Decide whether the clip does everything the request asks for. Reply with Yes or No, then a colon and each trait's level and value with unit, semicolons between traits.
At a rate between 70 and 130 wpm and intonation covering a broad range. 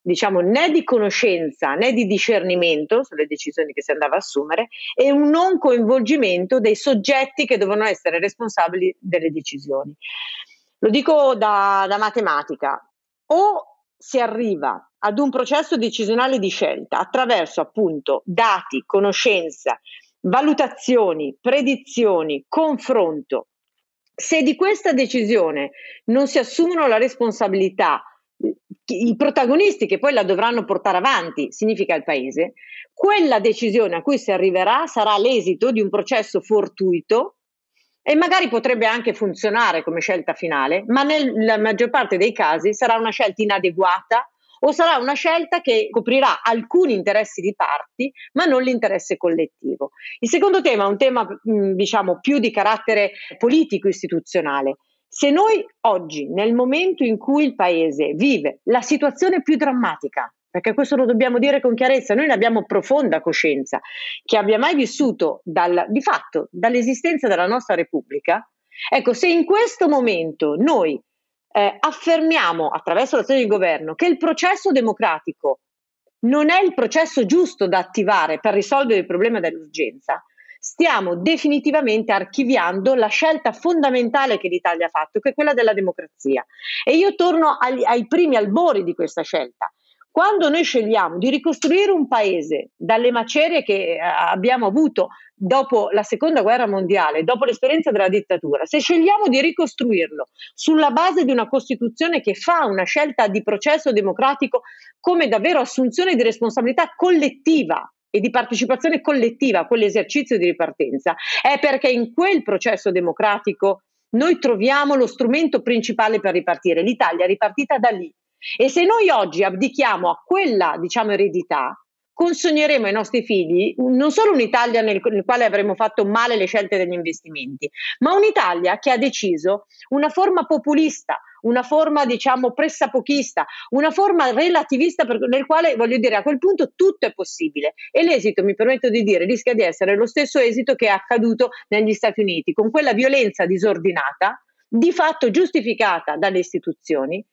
No: average, 145 wpm; wide, 7.0 semitones